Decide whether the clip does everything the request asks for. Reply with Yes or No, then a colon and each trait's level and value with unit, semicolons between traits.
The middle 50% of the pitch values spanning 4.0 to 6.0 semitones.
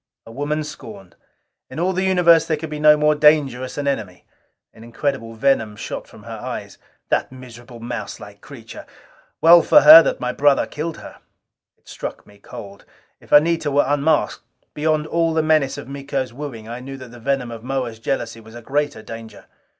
Yes: average, 4.7 semitones